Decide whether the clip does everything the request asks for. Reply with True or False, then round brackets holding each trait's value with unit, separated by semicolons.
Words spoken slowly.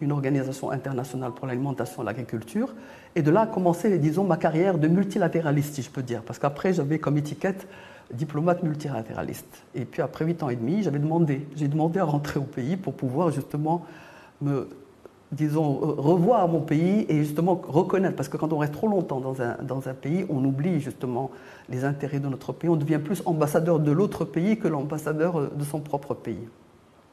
False (195 wpm)